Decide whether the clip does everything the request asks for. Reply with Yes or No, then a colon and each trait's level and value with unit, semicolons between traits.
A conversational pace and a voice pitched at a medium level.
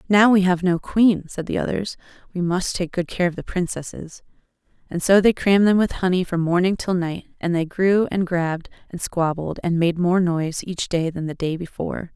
No: fast, 215 wpm; medium, 180 Hz